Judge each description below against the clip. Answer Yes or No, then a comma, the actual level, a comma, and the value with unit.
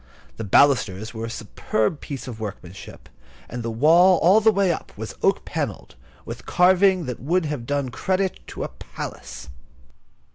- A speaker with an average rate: Yes, average, 160 wpm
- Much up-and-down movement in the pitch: Yes, wide, 8.1 semitones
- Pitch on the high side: No, medium, 140 Hz